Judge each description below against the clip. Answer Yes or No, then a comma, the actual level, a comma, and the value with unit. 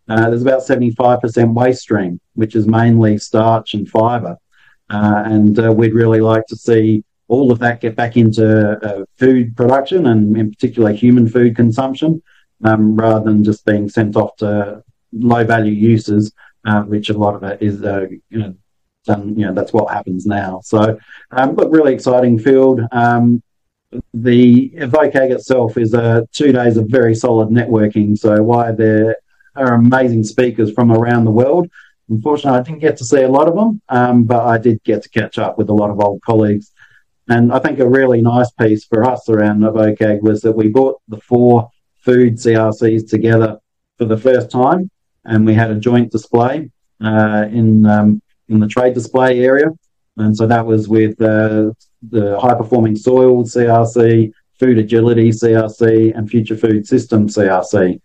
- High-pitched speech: No, low, 115 Hz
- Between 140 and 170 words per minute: No, average, 180 wpm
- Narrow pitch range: Yes, narrow, 2.3 semitones